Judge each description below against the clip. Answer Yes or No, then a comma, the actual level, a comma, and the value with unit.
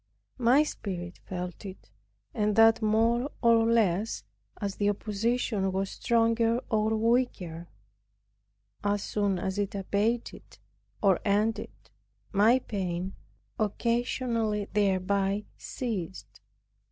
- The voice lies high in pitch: Yes, high, 210 Hz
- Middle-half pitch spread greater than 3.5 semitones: No, average, 3.0 semitones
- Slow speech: Yes, slow, 100 wpm